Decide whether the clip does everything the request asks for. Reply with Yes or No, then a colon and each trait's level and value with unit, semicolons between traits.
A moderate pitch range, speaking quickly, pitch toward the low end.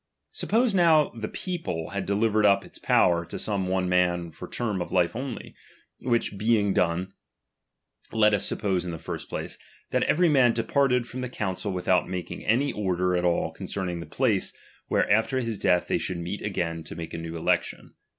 Yes: average, 4.8 semitones; fast, 210 wpm; low, 100 Hz